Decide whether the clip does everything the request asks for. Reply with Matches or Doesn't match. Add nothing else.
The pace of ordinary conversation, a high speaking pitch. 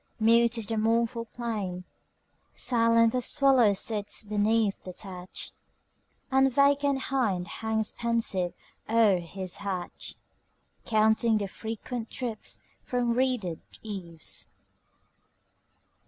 Doesn't match